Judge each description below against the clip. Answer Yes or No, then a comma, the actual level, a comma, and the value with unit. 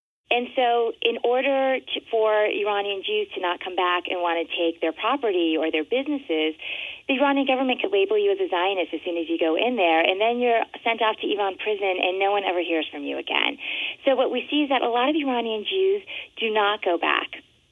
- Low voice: No, high, 220 Hz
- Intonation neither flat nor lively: No, wide, 7.1 semitones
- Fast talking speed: Yes, fast, 230 wpm